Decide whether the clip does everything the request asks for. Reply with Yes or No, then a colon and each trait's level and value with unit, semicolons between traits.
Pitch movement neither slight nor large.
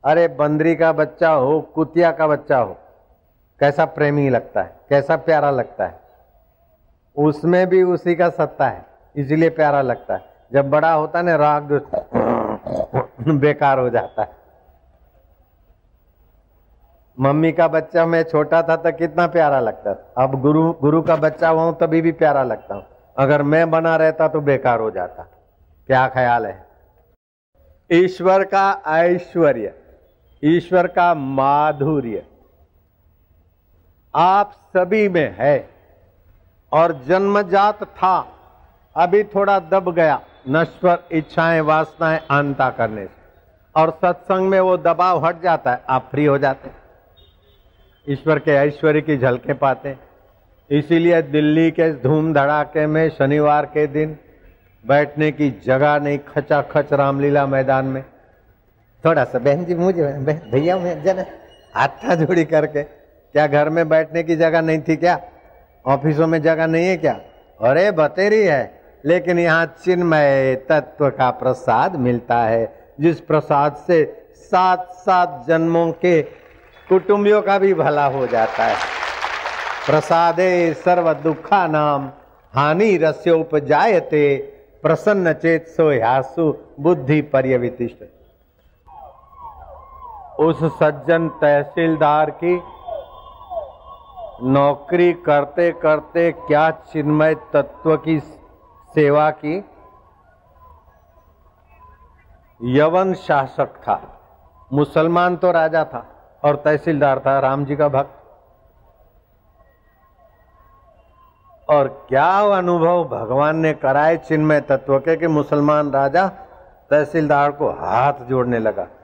Yes: average, 3.6 semitones